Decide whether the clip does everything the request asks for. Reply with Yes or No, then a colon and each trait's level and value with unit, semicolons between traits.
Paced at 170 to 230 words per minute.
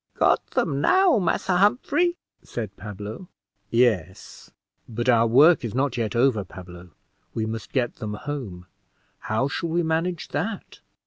No: average, 140 wpm